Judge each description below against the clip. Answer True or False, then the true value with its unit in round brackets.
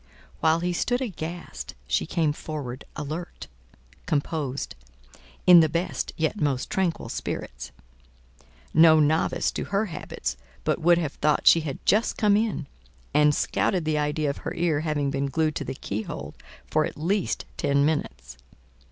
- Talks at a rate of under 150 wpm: False (155 wpm)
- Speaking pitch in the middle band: True (155 Hz)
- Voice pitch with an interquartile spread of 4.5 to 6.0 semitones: False (3.4 semitones)